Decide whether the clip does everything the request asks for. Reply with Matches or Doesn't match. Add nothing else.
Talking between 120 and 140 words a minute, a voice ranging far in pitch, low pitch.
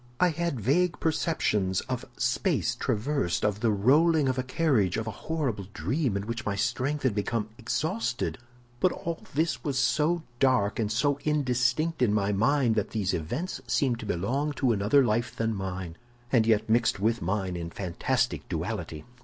Doesn't match